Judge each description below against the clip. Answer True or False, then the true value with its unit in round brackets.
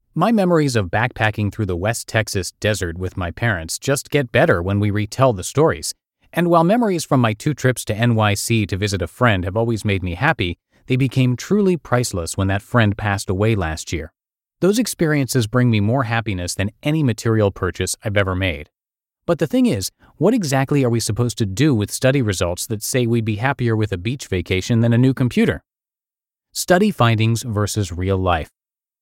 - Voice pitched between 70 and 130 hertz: True (115 Hz)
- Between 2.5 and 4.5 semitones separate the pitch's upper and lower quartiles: False (5.1 semitones)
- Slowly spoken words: False (195 wpm)